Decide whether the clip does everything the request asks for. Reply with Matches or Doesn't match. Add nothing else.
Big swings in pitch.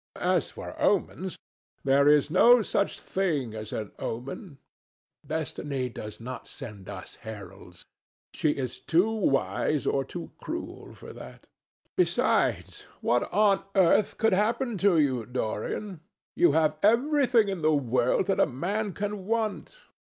Matches